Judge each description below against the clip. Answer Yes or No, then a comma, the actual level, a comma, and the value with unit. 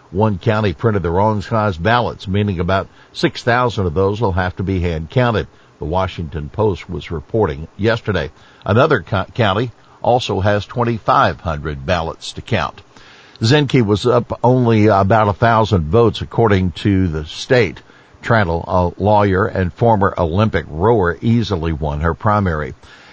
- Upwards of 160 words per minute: No, average, 155 wpm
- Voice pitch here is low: Yes, low, 100 Hz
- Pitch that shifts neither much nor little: Yes, average, 4.0 semitones